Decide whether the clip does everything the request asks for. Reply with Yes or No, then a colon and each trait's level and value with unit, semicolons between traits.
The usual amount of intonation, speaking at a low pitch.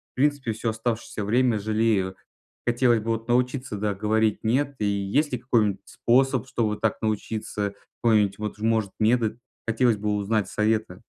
No: narrow, 2.2 semitones; low, 110 Hz